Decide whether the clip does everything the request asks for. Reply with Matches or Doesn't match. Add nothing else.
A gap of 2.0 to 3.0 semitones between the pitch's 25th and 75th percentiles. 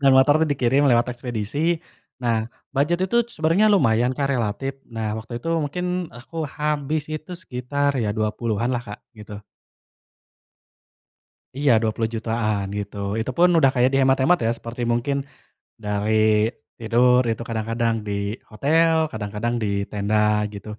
Doesn't match